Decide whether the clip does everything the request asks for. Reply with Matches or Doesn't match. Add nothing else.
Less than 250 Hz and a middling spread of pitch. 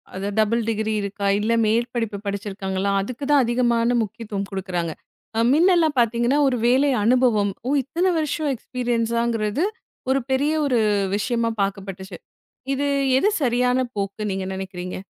Matches